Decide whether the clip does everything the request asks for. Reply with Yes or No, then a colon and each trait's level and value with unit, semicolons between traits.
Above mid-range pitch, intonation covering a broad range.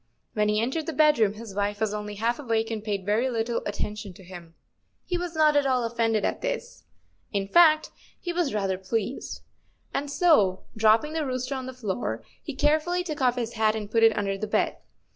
Yes: high, 230 Hz; wide, 6.0 semitones